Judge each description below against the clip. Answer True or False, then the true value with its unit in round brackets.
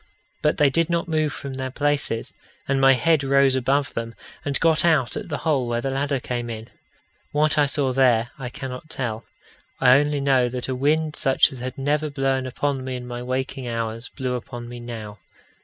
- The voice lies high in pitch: False (135 Hz)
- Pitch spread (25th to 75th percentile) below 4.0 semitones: True (2.8 semitones)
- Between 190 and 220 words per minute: True (205 wpm)